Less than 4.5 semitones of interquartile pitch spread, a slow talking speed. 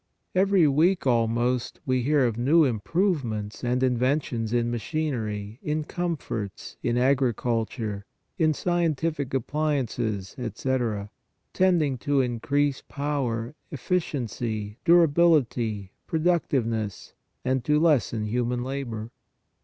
No: average, 4.8 semitones; slow, 105 wpm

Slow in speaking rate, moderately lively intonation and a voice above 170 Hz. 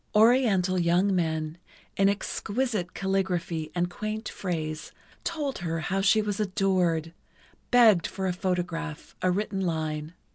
Yes: slow, 130 wpm; average, 3.4 semitones; medium, 185 Hz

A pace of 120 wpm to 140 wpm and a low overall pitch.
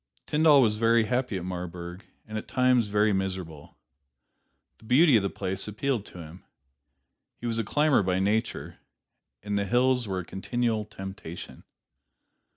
No: average, 155 wpm; low, 105 Hz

